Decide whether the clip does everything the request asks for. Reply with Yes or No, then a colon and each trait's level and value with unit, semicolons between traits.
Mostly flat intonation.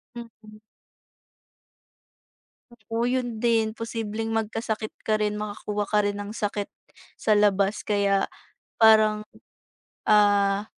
Yes: narrow, 1.5 semitones